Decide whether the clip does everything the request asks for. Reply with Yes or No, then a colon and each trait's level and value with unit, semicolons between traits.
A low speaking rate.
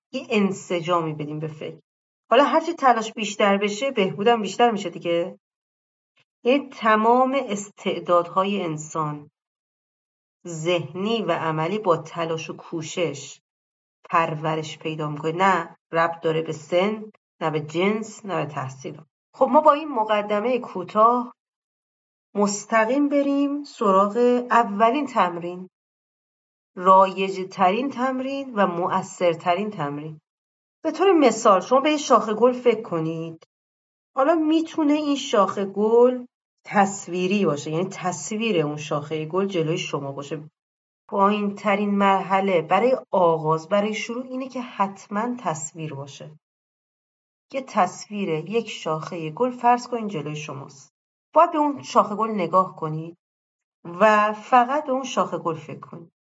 No: average, 125 wpm